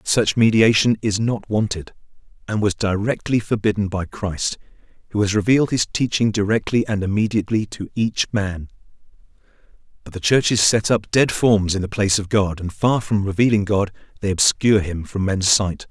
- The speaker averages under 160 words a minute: No, average, 170 wpm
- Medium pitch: No, low, 105 Hz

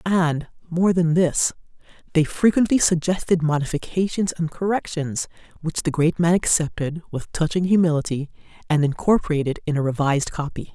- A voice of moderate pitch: Yes, medium, 165 Hz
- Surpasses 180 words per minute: No, slow, 135 wpm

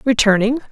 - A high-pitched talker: Yes, high, 235 Hz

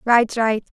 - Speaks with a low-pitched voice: No, high, 225 Hz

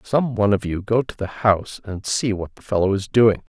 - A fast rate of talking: Yes, fast, 255 wpm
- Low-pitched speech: Yes, low, 105 Hz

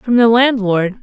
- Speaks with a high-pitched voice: Yes, high, 225 Hz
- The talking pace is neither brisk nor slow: Yes, average, 175 wpm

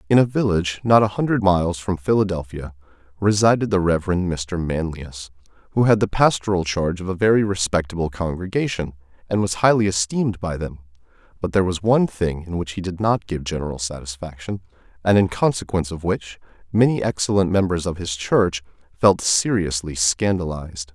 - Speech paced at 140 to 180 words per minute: Yes, average, 165 wpm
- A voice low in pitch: Yes, very low, 90 Hz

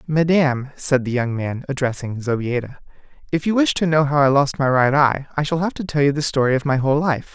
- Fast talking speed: Yes, fast, 245 wpm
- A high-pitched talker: No, medium, 140 Hz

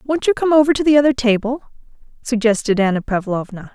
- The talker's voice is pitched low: No, high, 245 Hz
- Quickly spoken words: No, average, 175 wpm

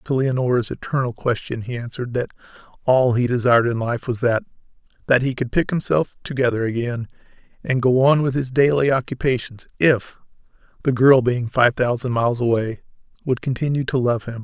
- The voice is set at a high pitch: No, low, 125 Hz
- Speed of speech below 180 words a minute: Yes, average, 160 wpm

